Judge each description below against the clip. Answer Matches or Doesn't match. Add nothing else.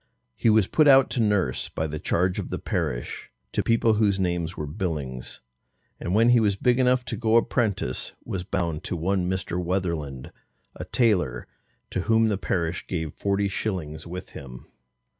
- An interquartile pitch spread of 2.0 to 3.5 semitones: Doesn't match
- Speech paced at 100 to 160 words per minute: Doesn't match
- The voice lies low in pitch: Matches